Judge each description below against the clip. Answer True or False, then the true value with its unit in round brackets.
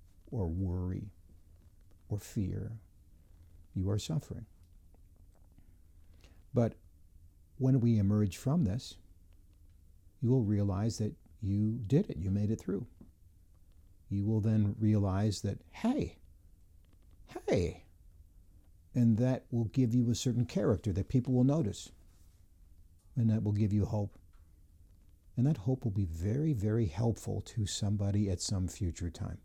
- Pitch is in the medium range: False (95 Hz)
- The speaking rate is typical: False (130 wpm)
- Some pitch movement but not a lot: True (4.2 semitones)